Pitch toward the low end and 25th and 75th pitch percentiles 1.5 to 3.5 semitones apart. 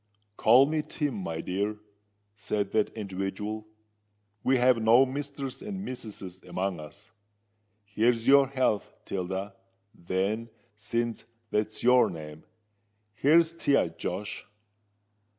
No: low, 110 Hz; average, 4.8 semitones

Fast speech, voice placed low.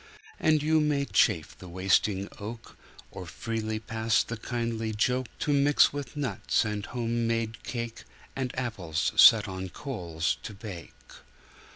No: average, 145 wpm; low, 115 Hz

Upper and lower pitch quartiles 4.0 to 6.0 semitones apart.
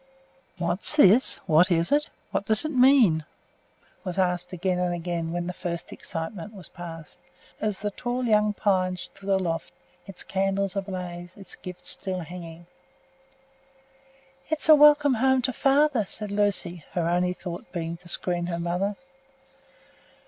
No: average, 3.4 semitones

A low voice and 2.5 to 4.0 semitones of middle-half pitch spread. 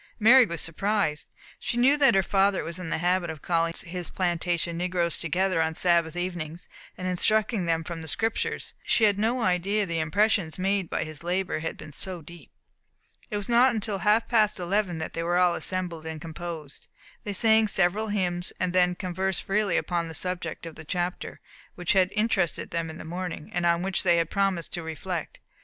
No: medium, 180 Hz; average, 2.9 semitones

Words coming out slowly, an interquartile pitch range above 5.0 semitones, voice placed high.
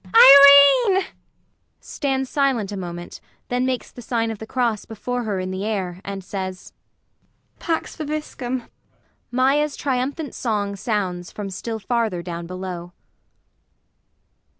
Yes: slow, 125 wpm; wide, 5.5 semitones; high, 225 Hz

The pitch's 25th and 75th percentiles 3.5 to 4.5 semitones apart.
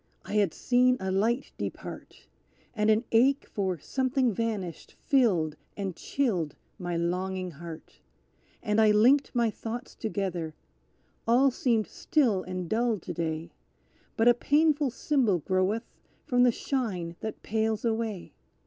No: average, 4.9 semitones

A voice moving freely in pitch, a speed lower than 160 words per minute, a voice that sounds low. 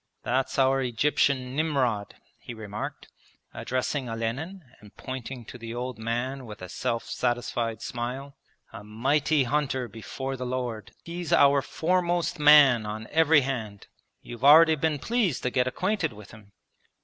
No: average, 4.3 semitones; average, 145 wpm; low, 130 Hz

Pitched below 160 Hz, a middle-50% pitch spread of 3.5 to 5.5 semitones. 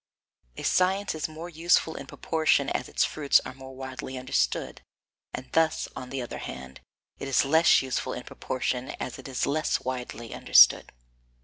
Yes: low, 135 Hz; average, 3.9 semitones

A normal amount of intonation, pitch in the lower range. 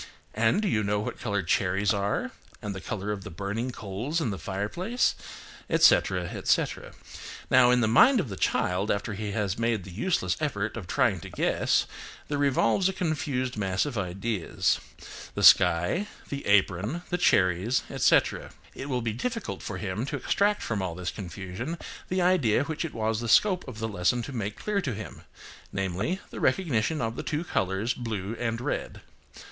No: wide, 6.3 semitones; low, 110 Hz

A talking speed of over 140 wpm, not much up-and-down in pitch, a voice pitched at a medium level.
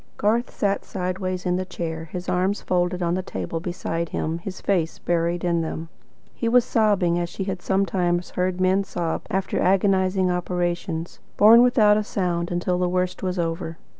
Yes: average, 175 wpm; narrow, 1.9 semitones; medium, 180 Hz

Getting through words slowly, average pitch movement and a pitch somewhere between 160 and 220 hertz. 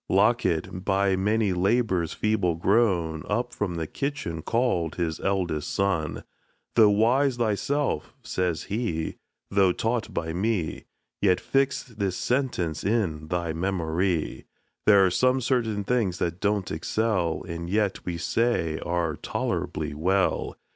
No: slow, 130 wpm; average, 4.9 semitones; very low, 95 Hz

